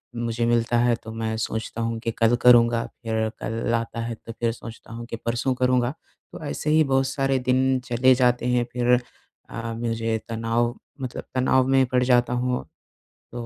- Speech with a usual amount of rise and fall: No, narrow, 1.7 semitones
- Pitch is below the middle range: Yes, low, 120 Hz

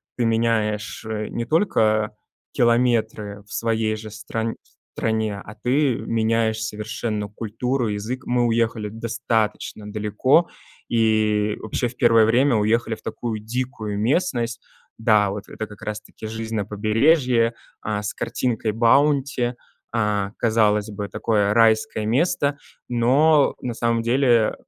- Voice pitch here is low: Yes, low, 110 Hz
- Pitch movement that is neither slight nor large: No, narrow, 2.0 semitones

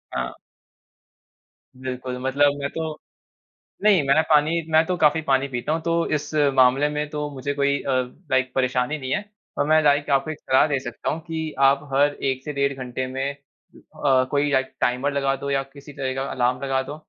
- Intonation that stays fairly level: Yes, narrow, 2.1 semitones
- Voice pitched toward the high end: No, medium, 140 Hz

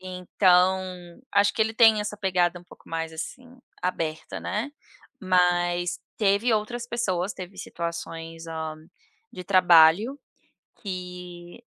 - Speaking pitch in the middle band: Yes, medium, 180 Hz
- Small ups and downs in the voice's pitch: No, average, 3.1 semitones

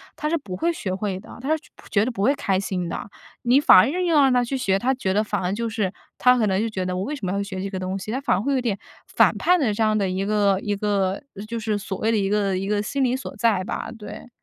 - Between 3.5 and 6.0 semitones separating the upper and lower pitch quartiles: Yes, average, 4.3 semitones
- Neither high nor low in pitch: No, high, 210 Hz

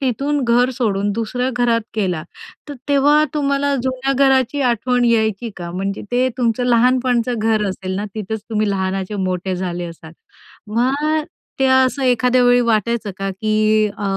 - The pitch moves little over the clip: No, average, 4.1 semitones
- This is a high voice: Yes, high, 235 Hz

